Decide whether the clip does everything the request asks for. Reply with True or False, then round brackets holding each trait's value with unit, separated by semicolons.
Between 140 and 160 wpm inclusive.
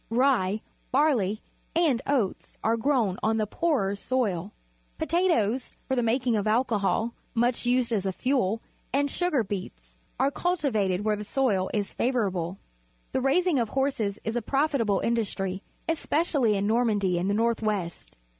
True (155 wpm)